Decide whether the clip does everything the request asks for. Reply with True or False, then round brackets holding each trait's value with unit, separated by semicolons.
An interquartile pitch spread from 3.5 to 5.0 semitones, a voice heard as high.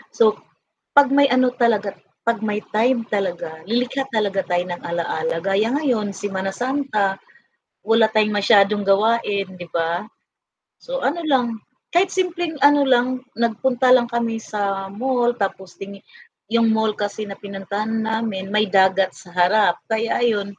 True (3.8 semitones; 215 Hz)